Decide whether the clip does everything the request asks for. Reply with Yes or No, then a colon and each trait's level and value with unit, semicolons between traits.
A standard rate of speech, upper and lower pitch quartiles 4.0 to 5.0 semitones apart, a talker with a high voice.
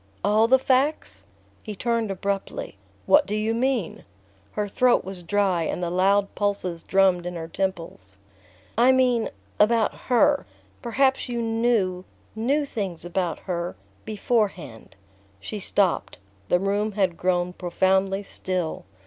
No: slow, 130 wpm; average, 4.4 semitones; high, 200 Hz